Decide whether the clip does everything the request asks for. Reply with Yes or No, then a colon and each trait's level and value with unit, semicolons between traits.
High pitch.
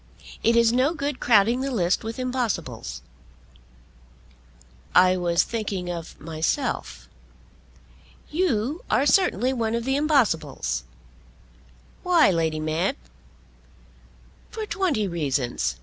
Yes: high, 225 Hz